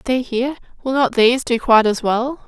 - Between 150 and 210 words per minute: No, fast, 245 wpm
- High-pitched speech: Yes, high, 245 Hz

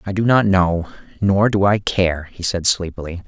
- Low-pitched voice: Yes, very low, 95 Hz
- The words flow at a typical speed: Yes, average, 185 wpm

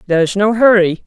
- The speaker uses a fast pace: Yes, fast, 225 wpm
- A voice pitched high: Yes, high, 200 Hz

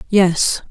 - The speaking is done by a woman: Yes, female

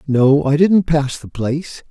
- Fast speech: No, average, 190 wpm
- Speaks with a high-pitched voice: No, medium, 145 Hz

